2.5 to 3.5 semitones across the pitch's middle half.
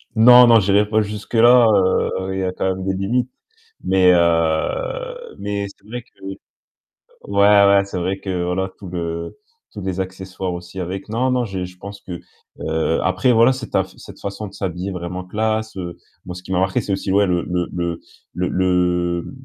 Yes: average, 2.9 semitones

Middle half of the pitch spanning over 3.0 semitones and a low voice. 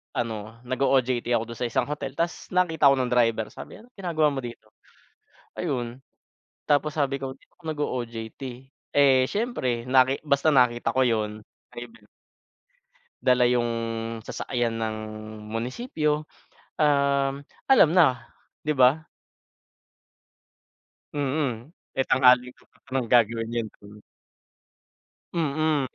Yes: average, 3.6 semitones; low, 130 Hz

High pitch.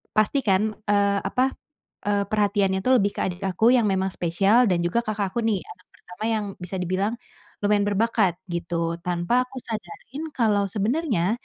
Yes: high, 205 Hz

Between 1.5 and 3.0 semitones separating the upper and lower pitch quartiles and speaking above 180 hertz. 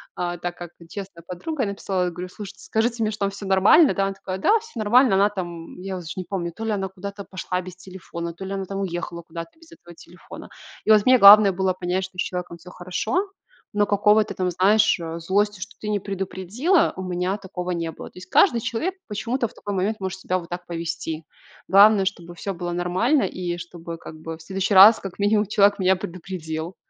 Yes: average, 2.7 semitones; high, 190 Hz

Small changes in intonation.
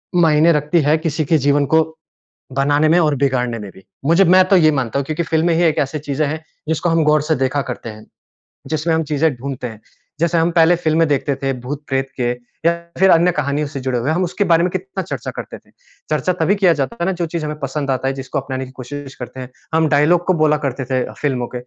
No: average, 3.4 semitones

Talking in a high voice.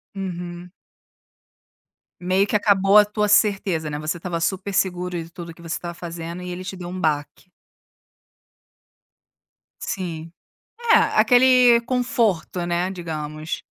No: medium, 180 Hz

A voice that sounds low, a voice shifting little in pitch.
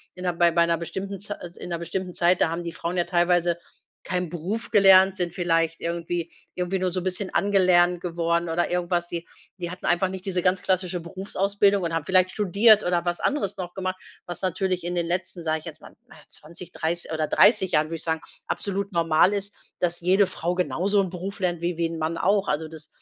No: medium, 175 Hz; narrow, 2.0 semitones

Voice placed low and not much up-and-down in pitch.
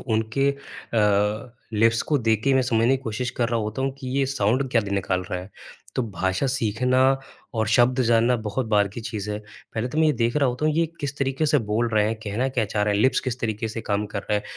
No: low, 115 Hz; average, 3.8 semitones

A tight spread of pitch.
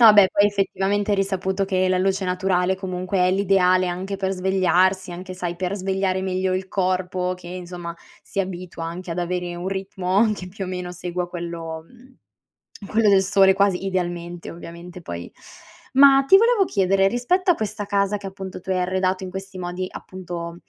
Yes: narrow, 1.4 semitones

